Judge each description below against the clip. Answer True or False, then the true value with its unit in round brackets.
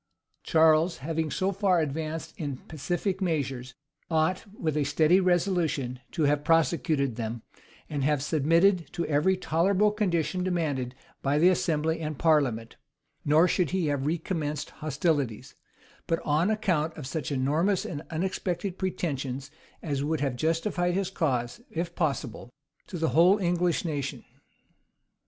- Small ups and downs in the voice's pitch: False (3.6 semitones)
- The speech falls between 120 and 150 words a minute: True (140 wpm)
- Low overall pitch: False (160 Hz)